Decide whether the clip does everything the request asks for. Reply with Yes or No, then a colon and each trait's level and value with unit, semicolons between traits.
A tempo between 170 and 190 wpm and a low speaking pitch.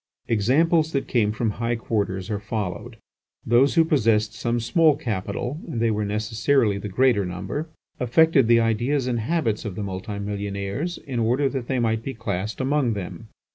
Yes: average, 175 wpm; low, 115 Hz